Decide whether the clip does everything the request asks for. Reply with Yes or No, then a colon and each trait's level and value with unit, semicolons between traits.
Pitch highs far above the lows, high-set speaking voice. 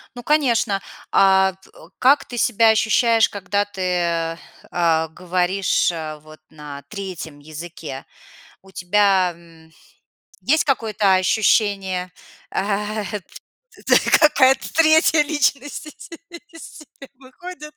Yes: wide, 7.0 semitones; high, 195 Hz